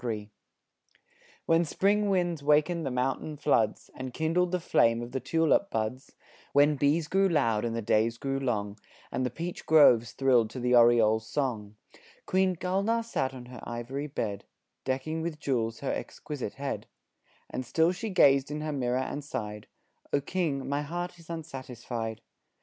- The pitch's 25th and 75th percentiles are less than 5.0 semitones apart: No, wide, 5.4 semitones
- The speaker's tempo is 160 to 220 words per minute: Yes, average, 165 wpm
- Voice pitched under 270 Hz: Yes, low, 135 Hz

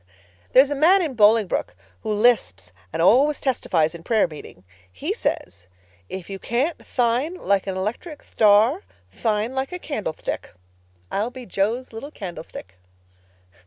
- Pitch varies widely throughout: Yes, wide, 6.0 semitones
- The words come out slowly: No, average, 145 wpm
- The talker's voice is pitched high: Yes, high, 220 Hz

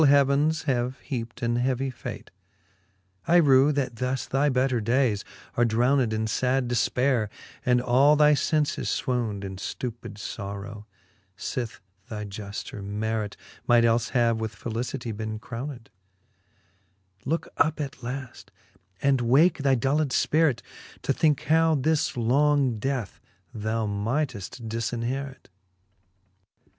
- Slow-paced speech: Yes, slow, 125 wpm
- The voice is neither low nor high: No, low, 125 Hz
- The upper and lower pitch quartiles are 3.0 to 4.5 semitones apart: Yes, average, 3.7 semitones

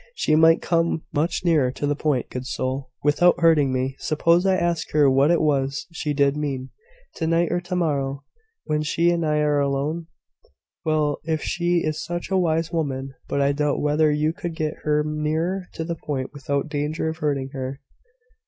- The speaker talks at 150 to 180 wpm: No, average, 190 wpm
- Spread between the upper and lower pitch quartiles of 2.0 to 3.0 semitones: Yes, average, 2.7 semitones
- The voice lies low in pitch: No, medium, 150 Hz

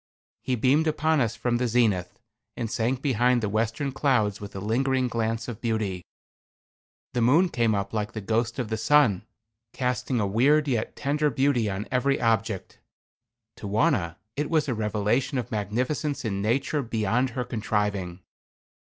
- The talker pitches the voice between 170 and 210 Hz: No, low, 115 Hz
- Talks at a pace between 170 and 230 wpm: No, average, 160 wpm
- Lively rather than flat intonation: No, average, 3.8 semitones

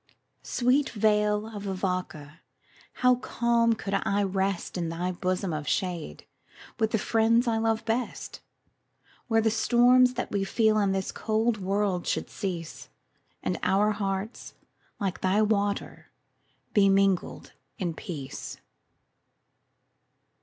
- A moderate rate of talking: No, slow, 125 wpm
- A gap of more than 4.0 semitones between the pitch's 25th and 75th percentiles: No, average, 3.2 semitones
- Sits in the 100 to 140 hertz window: No, high, 205 Hz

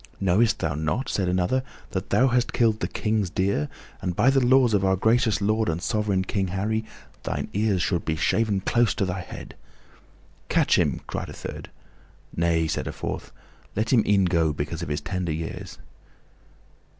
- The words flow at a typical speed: Yes, average, 180 wpm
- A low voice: Yes, very low, 95 Hz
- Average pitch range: Yes, average, 4.1 semitones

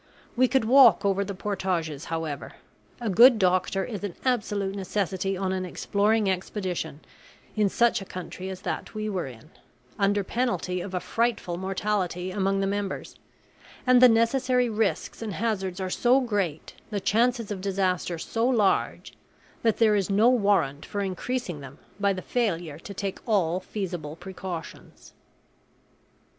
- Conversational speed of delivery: Yes, average, 150 wpm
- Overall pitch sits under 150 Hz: No, high, 195 Hz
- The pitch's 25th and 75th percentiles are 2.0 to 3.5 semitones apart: Yes, average, 3.2 semitones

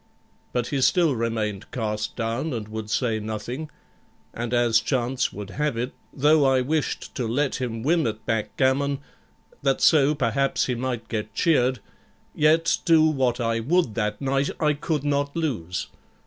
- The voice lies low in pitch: Yes, low, 130 Hz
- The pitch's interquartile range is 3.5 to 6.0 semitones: Yes, average, 4.3 semitones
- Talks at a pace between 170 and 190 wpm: No, average, 160 wpm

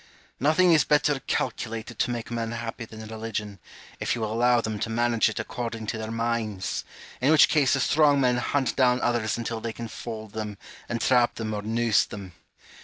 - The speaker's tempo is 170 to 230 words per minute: Yes, average, 190 wpm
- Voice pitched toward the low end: Yes, low, 115 Hz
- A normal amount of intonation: No, narrow, 2.0 semitones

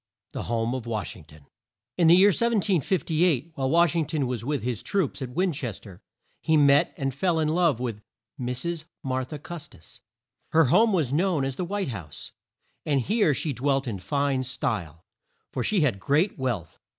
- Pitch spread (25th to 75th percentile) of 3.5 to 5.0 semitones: No, wide, 5.6 semitones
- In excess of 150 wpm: Yes, average, 190 wpm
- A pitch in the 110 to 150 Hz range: Yes, medium, 140 Hz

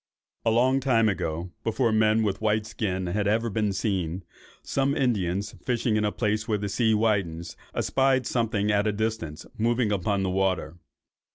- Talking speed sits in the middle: Yes, average, 175 wpm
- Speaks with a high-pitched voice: No, low, 105 Hz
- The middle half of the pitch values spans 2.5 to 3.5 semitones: Yes, average, 2.8 semitones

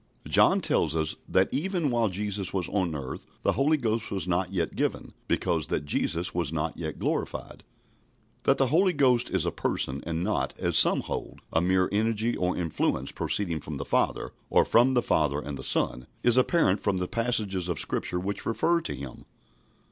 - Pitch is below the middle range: Yes, very low, 95 Hz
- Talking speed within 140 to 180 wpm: No, average, 190 wpm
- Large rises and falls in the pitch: Yes, wide, 6.3 semitones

